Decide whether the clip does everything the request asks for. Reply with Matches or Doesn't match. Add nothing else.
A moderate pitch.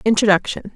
Doesn't match